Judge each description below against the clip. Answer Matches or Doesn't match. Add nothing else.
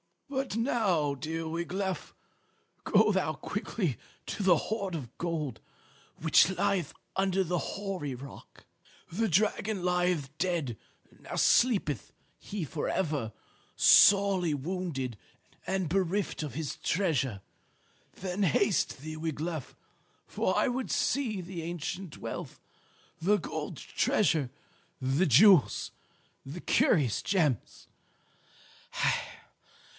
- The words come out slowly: Matches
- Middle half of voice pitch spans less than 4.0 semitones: Doesn't match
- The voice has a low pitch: Doesn't match